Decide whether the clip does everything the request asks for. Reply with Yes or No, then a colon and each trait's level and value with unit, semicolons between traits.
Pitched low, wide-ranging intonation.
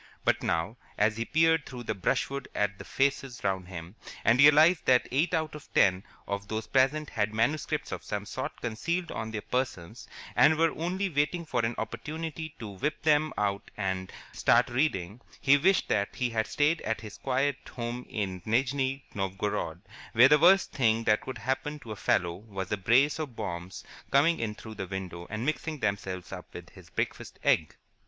Yes: low, 120 Hz; wide, 6.4 semitones